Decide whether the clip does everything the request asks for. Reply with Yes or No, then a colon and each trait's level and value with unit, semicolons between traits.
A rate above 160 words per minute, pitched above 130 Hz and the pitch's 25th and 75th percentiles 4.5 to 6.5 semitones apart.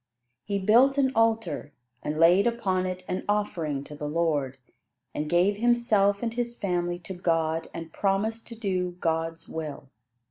No: average, 155 wpm; medium, 185 Hz; average, 5.1 semitones